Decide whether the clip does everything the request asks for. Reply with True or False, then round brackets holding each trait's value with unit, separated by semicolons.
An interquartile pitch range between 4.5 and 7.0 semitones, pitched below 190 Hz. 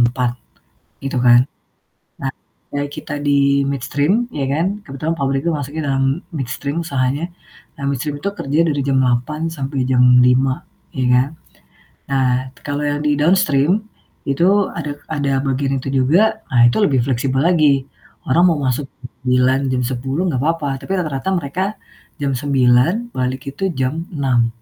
False (2.8 semitones; 140 Hz)